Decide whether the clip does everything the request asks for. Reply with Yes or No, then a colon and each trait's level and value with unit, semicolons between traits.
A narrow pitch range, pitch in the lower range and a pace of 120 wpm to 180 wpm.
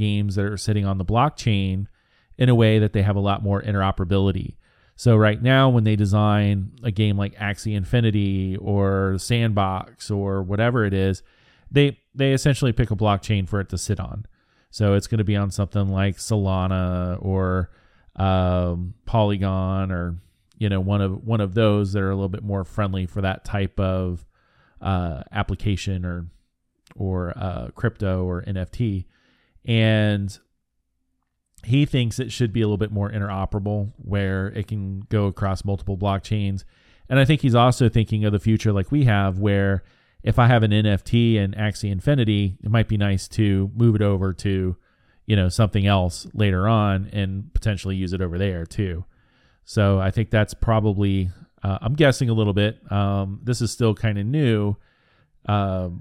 Yes: narrow, 2.2 semitones; low, 100 Hz; average, 175 wpm